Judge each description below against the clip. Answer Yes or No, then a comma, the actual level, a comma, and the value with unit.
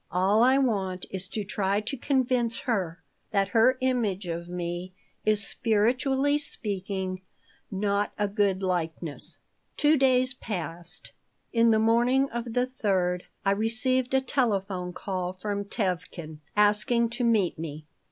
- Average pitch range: Yes, average, 4.7 semitones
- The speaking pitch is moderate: No, high, 205 Hz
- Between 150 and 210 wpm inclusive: No, slow, 135 wpm